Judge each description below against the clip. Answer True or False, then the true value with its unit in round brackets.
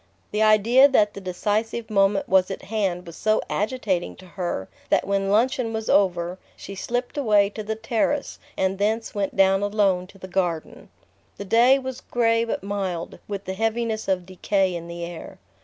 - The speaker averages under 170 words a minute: False (180 wpm)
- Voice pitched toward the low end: False (200 Hz)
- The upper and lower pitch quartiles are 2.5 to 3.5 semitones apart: True (3.0 semitones)